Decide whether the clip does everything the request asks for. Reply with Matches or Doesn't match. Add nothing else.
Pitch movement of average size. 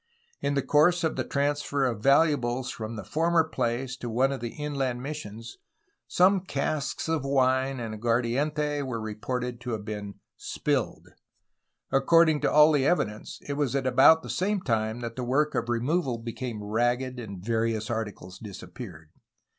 Matches